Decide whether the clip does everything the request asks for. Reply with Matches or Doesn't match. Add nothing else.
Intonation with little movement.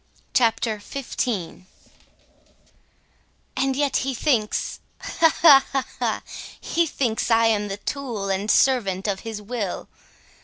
Doesn't match